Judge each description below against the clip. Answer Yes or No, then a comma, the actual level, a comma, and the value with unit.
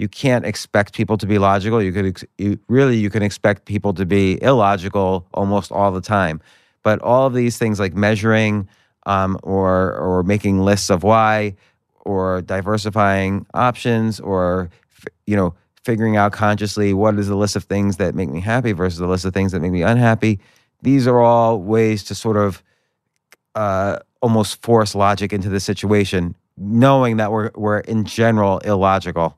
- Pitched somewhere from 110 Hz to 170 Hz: No, low, 100 Hz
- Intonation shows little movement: Yes, narrow, 2.3 semitones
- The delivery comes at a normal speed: Yes, average, 180 wpm